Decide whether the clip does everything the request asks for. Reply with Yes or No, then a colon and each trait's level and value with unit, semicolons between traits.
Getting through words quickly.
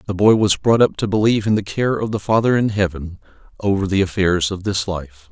Yes: fast, 235 wpm